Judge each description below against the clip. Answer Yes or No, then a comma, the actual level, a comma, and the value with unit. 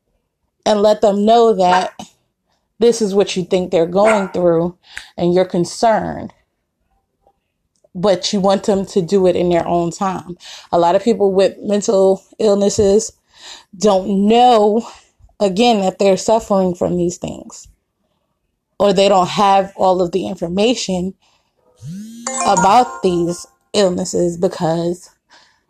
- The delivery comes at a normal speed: No, slow, 130 wpm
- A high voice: Yes, high, 195 Hz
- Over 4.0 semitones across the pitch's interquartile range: No, narrow, 2.6 semitones